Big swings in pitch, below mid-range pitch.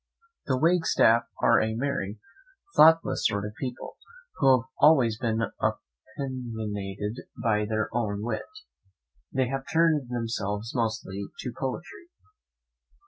No: average, 3.7 semitones; low, 115 Hz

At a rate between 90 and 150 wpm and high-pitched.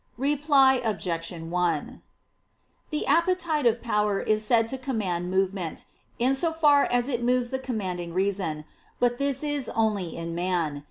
Yes: average, 145 wpm; high, 225 Hz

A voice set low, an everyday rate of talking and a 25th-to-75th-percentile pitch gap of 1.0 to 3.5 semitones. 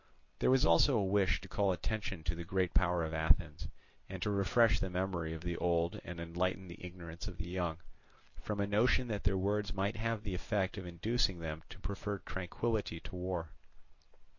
Yes: very low, 95 Hz; average, 195 wpm; average, 3.0 semitones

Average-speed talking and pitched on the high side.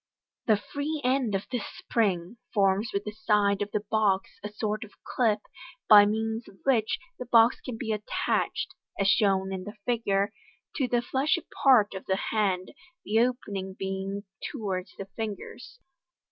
Yes: average, 160 wpm; high, 210 Hz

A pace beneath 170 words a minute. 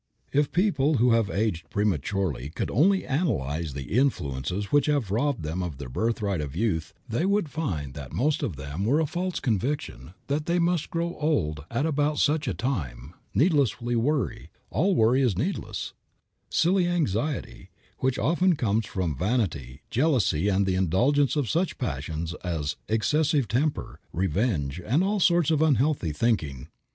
Yes: average, 160 wpm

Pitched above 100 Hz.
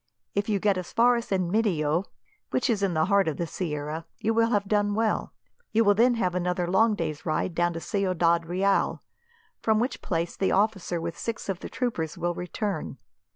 Yes: high, 190 Hz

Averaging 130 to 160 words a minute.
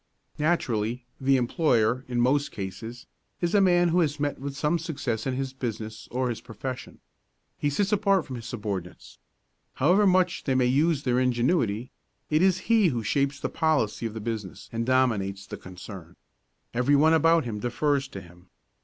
No: average, 175 wpm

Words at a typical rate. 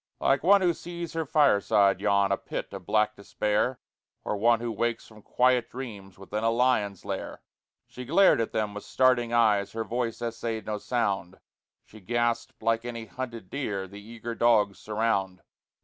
Yes: average, 170 wpm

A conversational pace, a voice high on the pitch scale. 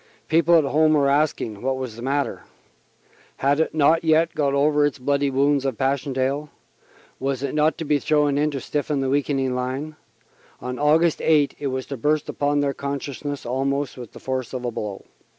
No: average, 195 wpm; medium, 140 Hz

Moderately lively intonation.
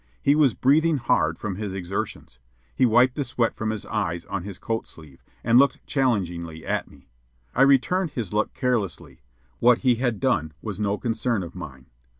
No: wide, 5.8 semitones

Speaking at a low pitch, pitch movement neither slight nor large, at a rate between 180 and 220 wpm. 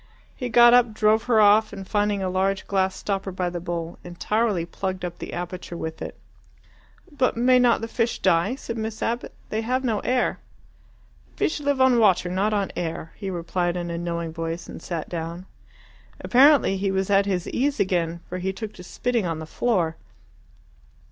No: high, 195 Hz; average, 4.5 semitones; average, 190 wpm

